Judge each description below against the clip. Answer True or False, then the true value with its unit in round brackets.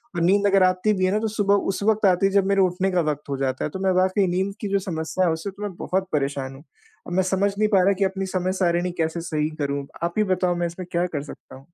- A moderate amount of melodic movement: True (3.3 semitones)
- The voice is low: False (185 Hz)